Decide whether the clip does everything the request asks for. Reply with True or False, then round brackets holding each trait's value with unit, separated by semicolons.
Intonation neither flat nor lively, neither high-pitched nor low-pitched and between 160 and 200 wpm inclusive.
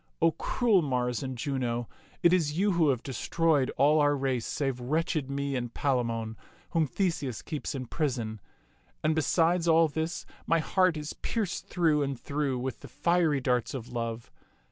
True (4.5 semitones; 145 Hz; 165 wpm)